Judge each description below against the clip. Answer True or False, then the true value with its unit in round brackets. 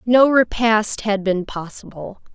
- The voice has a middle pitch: False (215 Hz)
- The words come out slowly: True (130 wpm)